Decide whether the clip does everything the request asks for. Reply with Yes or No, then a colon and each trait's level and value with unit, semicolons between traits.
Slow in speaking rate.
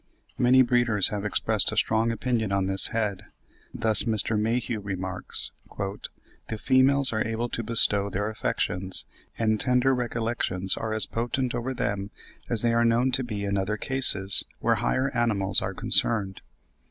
No: average, 155 wpm